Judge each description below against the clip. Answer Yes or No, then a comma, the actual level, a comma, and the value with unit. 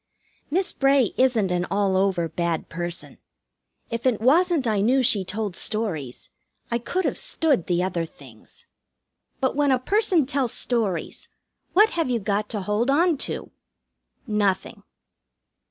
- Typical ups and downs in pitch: No, wide, 6.3 semitones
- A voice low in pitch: No, high, 225 Hz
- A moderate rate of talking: Yes, average, 145 wpm